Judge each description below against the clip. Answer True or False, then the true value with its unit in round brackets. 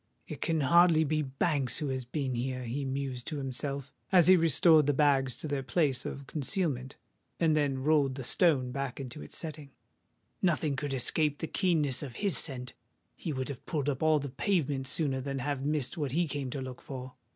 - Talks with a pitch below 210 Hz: True (140 Hz)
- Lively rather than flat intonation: False (2.8 semitones)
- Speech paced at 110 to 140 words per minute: False (200 wpm)